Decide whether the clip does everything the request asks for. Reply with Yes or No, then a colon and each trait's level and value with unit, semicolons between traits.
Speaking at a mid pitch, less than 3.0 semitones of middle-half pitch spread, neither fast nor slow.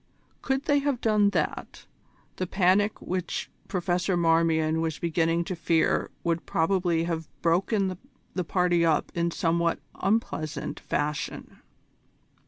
No: medium, 170 Hz; narrow, 2.6 semitones; slow, 120 wpm